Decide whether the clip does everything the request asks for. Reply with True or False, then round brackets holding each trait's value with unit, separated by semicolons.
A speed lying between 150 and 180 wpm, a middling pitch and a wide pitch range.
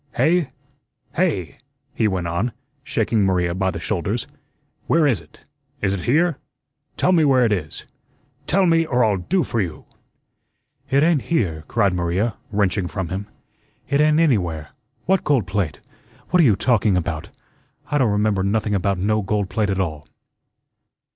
False (160 wpm; 105 Hz; 6.8 semitones)